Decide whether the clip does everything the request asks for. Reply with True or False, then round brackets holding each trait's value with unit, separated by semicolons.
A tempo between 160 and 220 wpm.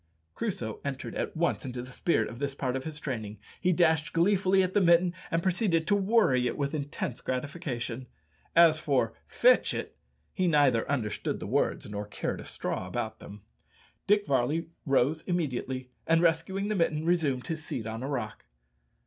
True (175 wpm)